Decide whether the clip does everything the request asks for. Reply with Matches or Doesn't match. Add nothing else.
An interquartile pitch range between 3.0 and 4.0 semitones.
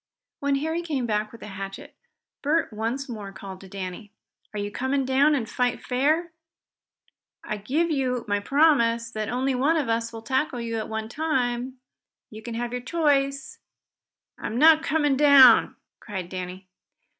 Doesn't match